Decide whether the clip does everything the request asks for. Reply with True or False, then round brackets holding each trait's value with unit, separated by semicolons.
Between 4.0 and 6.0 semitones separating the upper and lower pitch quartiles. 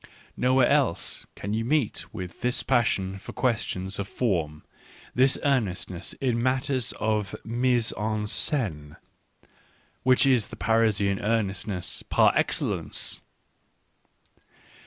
True (4.6 semitones)